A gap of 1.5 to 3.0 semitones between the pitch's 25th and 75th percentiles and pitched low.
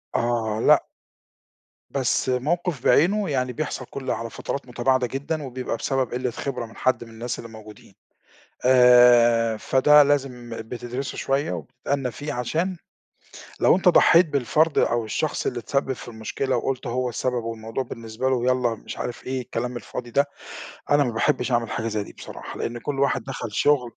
Yes: average, 2.7 semitones; low, 125 Hz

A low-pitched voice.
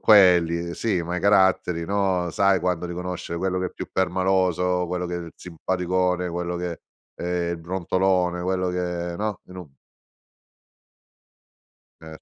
Yes: very low, 90 Hz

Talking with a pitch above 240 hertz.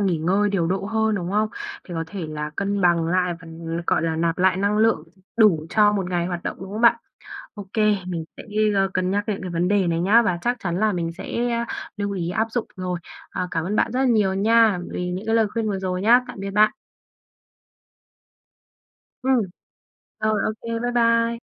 No: high, 195 Hz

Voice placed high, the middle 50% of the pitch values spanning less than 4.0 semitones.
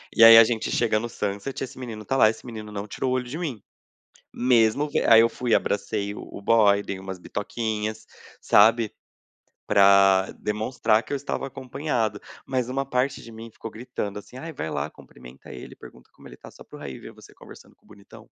No: low, 110 Hz; average, 3.6 semitones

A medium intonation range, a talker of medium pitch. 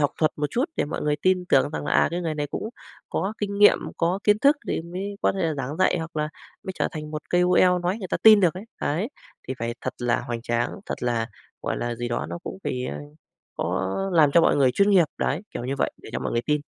No: wide, 5.7 semitones; medium, 155 Hz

